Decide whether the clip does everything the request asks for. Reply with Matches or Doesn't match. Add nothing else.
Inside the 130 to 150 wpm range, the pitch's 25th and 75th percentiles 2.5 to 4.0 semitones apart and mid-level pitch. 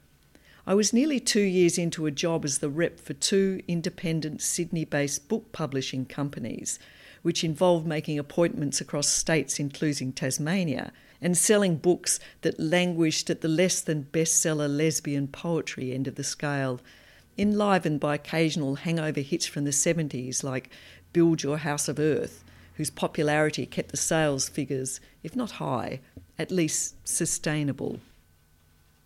Matches